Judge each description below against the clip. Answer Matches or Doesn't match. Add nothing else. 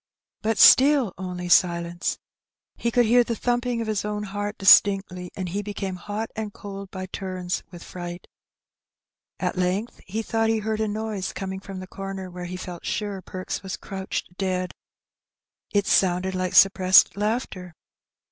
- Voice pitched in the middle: Doesn't match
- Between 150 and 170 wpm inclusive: Matches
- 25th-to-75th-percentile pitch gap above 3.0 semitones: Doesn't match